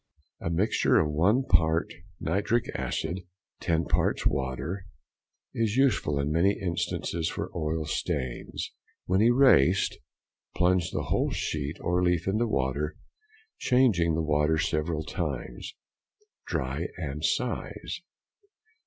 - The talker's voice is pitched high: No, very low, 85 Hz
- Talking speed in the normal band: No, slow, 115 wpm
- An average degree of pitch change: Yes, average, 4.0 semitones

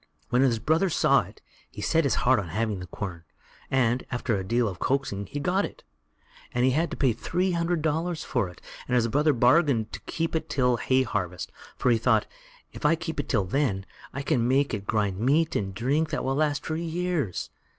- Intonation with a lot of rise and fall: Yes, wide, 6.0 semitones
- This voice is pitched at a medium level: No, low, 130 Hz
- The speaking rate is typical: No, fast, 215 wpm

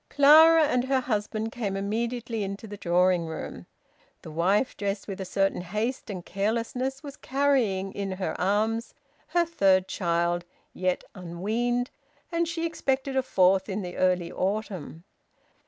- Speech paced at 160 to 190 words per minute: No, average, 145 wpm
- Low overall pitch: No, high, 205 Hz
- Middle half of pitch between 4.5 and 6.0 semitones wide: Yes, average, 5.2 semitones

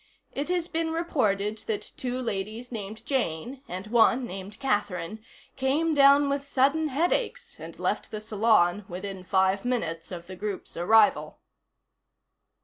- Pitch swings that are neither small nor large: No, wide, 6.1 semitones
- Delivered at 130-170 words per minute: Yes, average, 140 wpm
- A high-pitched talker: Yes, high, 225 Hz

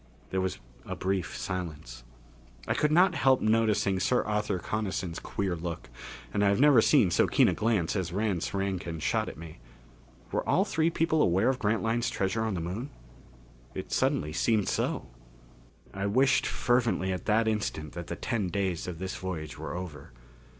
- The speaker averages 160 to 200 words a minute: Yes, average, 175 wpm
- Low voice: Yes, low, 100 Hz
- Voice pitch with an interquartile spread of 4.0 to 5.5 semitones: Yes, average, 4.3 semitones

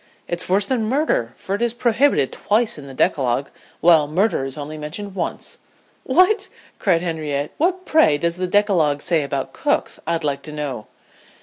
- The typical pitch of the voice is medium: Yes, medium, 170 Hz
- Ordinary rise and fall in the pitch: No, wide, 6.3 semitones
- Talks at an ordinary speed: Yes, average, 175 wpm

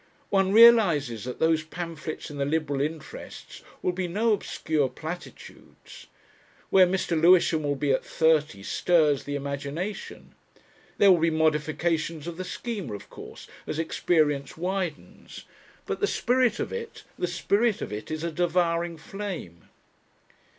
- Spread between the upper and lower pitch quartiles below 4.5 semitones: Yes, average, 3.8 semitones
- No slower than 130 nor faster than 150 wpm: Yes, average, 145 wpm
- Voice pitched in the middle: Yes, medium, 165 Hz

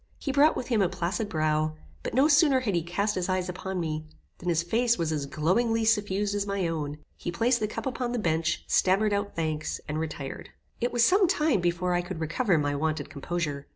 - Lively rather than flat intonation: Yes, wide, 6.0 semitones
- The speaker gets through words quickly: Yes, fast, 220 wpm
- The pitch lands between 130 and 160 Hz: No, medium, 185 Hz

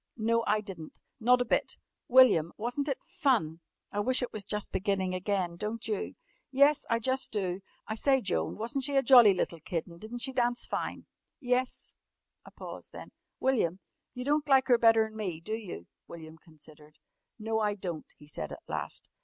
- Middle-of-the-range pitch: No, high, 220 Hz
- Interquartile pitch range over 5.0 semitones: Yes, wide, 5.4 semitones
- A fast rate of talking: No, average, 185 wpm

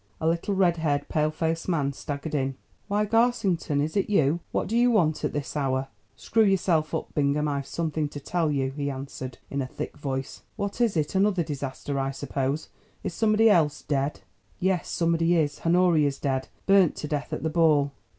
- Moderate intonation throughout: Yes, average, 4.1 semitones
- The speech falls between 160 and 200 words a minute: Yes, average, 190 wpm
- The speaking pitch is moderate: Yes, medium, 155 Hz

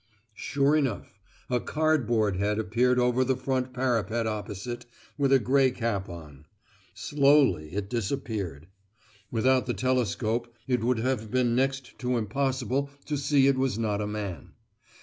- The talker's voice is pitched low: Yes, low, 125 Hz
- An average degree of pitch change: Yes, average, 3.8 semitones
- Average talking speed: Yes, average, 145 wpm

